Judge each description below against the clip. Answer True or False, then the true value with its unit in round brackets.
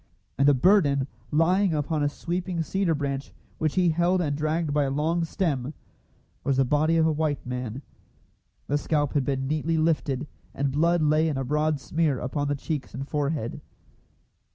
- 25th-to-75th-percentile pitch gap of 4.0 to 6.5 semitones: False (2.7 semitones)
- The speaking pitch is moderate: True (150 Hz)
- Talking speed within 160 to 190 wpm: True (175 wpm)